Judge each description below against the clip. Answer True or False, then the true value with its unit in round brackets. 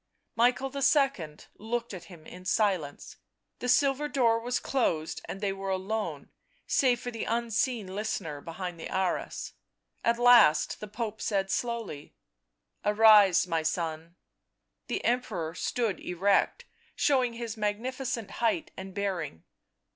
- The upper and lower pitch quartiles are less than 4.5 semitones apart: False (4.8 semitones)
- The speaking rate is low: True (130 wpm)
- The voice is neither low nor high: False (215 Hz)